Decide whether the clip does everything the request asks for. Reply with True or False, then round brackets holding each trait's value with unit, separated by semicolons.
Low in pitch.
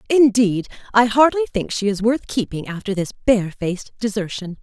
False (215 Hz)